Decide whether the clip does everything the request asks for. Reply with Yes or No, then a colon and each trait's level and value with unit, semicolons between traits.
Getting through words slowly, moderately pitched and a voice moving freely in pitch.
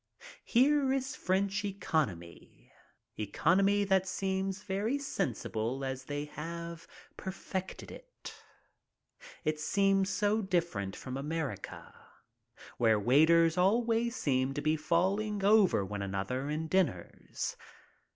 Yes: slow, 110 wpm; medium, 170 Hz; wide, 6.5 semitones